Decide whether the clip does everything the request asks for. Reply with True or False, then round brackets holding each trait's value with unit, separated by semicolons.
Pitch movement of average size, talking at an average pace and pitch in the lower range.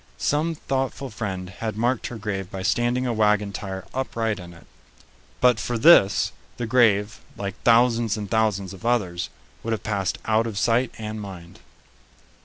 True (3.3 semitones; 165 wpm; 110 Hz)